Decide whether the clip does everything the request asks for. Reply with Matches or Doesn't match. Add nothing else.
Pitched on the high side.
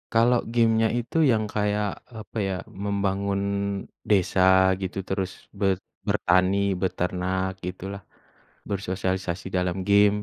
Doesn't match